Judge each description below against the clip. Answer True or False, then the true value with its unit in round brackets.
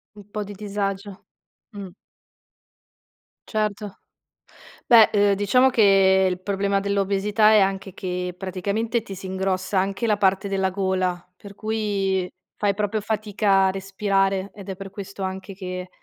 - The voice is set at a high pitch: True (195 Hz)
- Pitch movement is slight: True (1.4 semitones)